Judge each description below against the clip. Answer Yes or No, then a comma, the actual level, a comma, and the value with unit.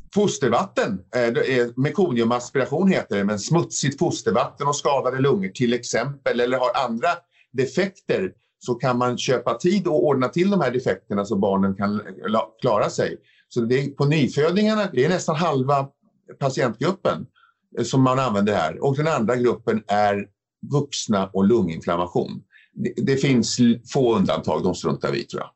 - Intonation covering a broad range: Yes, wide, 6.1 semitones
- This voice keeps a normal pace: Yes, average, 150 wpm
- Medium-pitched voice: No, low, 130 Hz